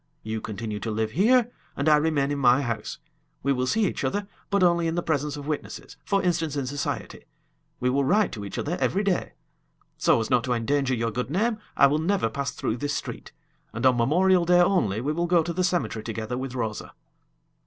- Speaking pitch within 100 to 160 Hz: Yes, medium, 140 Hz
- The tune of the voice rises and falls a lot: Yes, wide, 6.7 semitones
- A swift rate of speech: Yes, fast, 215 wpm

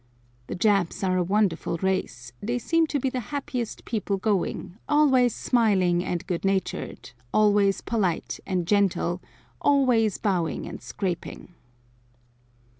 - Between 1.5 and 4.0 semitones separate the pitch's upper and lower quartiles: No, average, 4.6 semitones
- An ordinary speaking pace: No, slow, 125 wpm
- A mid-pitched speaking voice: No, high, 200 Hz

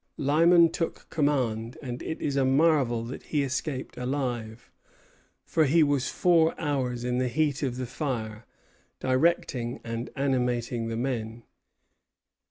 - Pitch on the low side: Yes, low, 130 Hz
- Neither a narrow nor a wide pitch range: Yes, average, 3.5 semitones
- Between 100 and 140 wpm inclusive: Yes, slow, 135 wpm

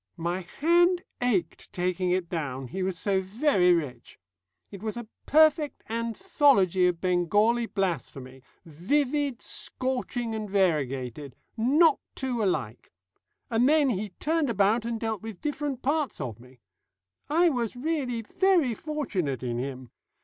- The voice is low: No, high, 215 Hz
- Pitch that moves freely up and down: Yes, wide, 7.9 semitones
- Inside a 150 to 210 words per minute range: No, slow, 135 wpm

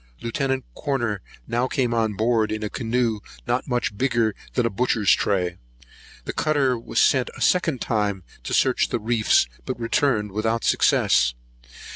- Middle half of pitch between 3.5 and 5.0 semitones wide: No, average, 2.8 semitones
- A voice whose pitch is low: Yes, low, 115 Hz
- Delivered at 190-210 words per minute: No, average, 155 wpm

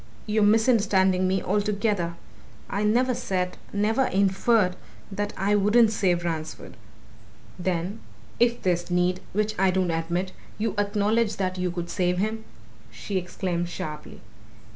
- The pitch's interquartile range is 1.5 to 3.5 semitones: Yes, average, 2.8 semitones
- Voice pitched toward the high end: Yes, high, 195 Hz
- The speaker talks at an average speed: No, slow, 130 wpm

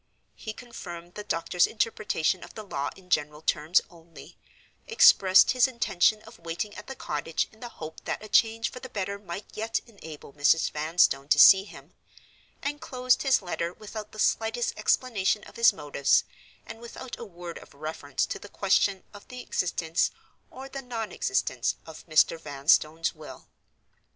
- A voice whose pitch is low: No, high, 190 Hz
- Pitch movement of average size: No, wide, 5.8 semitones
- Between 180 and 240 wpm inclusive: No, average, 170 wpm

